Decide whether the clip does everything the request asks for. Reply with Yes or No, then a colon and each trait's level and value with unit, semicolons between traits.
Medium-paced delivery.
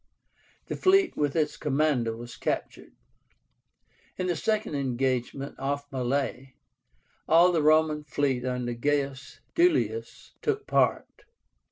No: slow, 115 wpm